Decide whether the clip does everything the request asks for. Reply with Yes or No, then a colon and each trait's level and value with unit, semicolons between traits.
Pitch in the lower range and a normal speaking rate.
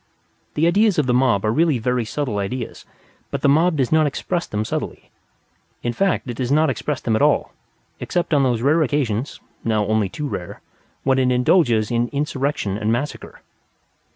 Yes: low, 130 Hz; average, 180 wpm